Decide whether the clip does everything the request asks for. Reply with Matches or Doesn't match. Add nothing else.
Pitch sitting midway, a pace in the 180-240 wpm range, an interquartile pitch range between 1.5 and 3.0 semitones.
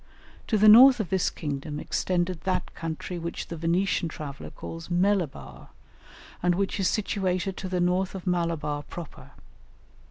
Doesn't match